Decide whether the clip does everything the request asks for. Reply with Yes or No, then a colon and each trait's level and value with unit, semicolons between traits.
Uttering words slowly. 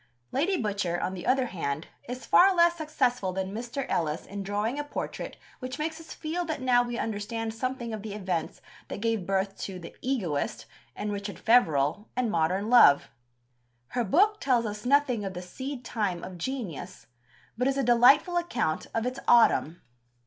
No: average, 180 wpm